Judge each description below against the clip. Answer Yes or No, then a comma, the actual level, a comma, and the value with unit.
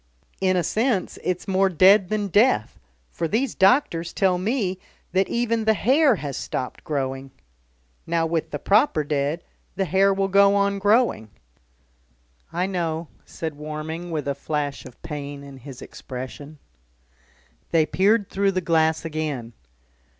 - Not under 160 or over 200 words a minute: No, average, 150 wpm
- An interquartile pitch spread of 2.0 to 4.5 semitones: No, average, 5.2 semitones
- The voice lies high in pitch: No, medium, 170 Hz